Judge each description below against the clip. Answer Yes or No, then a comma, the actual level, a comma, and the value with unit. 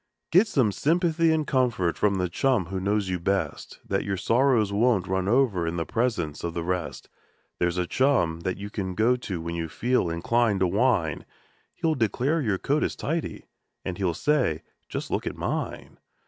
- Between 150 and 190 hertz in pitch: No, low, 100 Hz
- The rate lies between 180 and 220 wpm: Yes, average, 190 wpm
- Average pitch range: No, wide, 6.2 semitones